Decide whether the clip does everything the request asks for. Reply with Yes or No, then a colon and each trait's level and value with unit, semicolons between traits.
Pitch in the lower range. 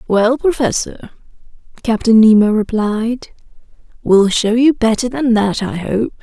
No: high, 225 Hz